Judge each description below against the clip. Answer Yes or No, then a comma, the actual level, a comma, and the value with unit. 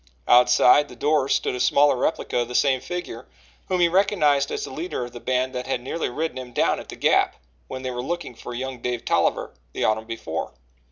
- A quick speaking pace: Yes, fast, 220 wpm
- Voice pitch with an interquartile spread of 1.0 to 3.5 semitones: Yes, average, 3.2 semitones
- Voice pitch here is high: No, low, 130 Hz